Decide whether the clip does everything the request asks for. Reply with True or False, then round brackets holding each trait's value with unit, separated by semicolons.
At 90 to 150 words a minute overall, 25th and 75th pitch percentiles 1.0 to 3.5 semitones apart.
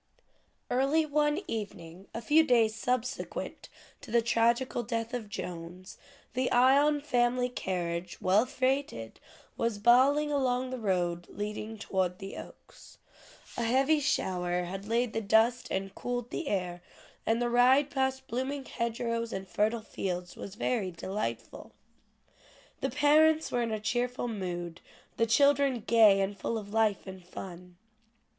False (140 wpm; 4.9 semitones)